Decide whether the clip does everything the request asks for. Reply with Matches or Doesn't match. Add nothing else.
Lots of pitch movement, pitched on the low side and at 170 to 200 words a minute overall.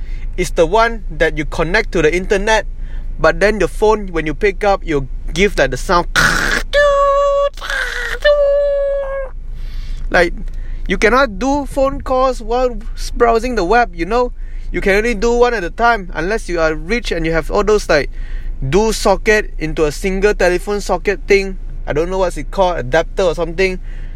Doesn't match